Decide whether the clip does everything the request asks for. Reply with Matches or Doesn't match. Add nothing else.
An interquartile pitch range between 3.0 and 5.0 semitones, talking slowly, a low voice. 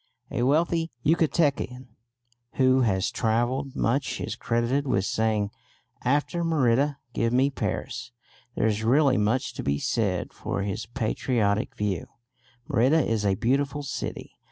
Matches